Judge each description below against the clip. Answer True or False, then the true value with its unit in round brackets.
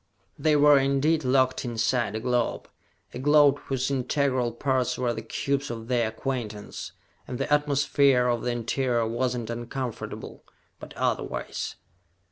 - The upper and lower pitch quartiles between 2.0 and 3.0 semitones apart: True (2.7 semitones)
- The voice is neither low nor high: False (125 Hz)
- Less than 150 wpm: True (140 wpm)